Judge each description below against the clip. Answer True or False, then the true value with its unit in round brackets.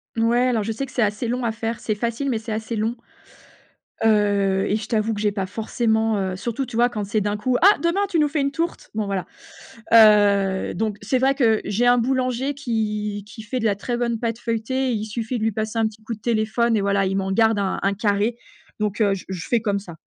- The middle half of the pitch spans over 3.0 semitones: False (2.6 semitones)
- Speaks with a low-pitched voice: False (220 Hz)